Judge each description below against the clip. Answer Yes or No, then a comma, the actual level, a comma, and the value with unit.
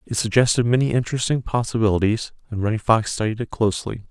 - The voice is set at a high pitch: No, low, 115 Hz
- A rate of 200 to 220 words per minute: No, average, 160 wpm